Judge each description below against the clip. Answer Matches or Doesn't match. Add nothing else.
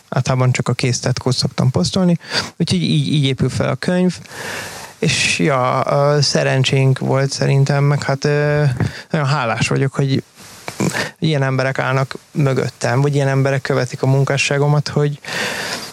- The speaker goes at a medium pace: Matches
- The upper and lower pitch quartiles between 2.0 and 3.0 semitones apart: Doesn't match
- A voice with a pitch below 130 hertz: Doesn't match